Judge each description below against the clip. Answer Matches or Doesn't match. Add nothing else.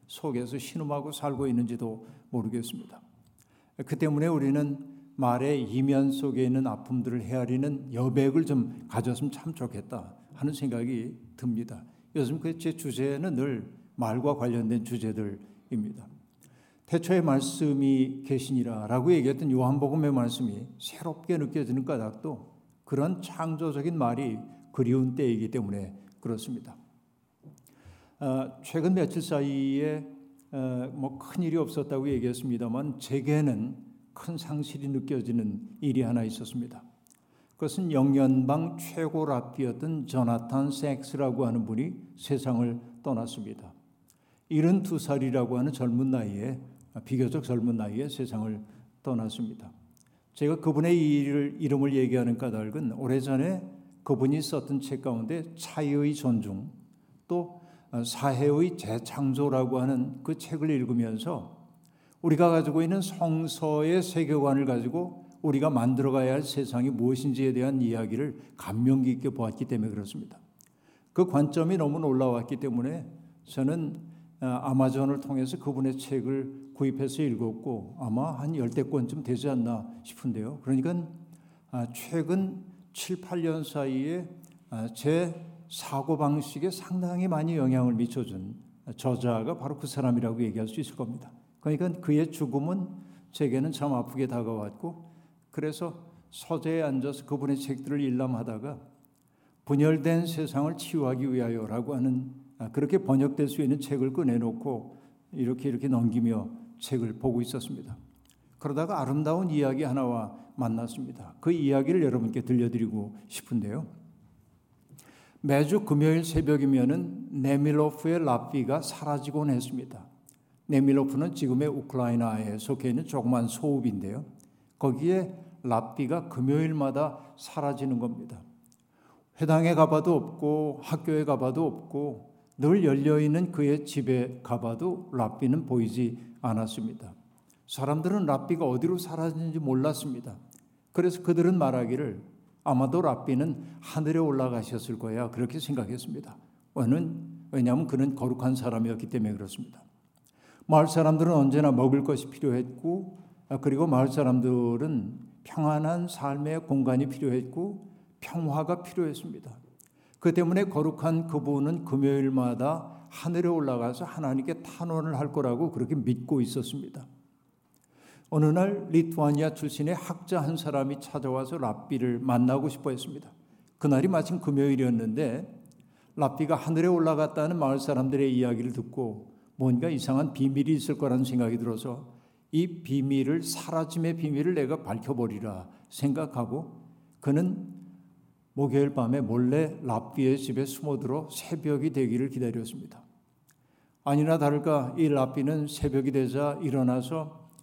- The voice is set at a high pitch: Doesn't match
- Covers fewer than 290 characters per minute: Doesn't match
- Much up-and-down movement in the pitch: Doesn't match